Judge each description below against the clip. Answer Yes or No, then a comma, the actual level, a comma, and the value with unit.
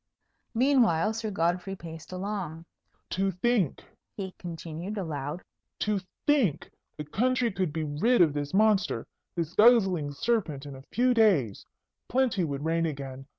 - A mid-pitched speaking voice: Yes, medium, 180 Hz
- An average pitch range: No, wide, 5.9 semitones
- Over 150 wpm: No, average, 140 wpm